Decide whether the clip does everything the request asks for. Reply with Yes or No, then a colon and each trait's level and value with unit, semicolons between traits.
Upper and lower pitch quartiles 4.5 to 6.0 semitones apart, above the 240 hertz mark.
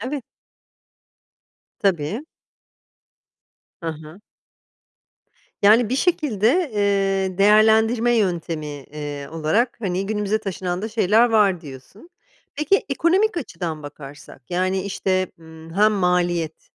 No: average, 5.2 semitones; high, 195 Hz